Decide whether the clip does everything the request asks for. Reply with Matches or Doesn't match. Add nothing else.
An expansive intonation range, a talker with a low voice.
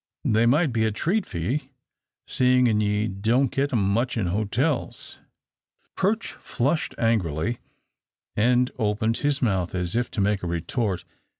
Doesn't match